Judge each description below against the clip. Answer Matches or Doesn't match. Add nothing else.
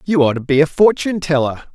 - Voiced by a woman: Doesn't match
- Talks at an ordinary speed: Doesn't match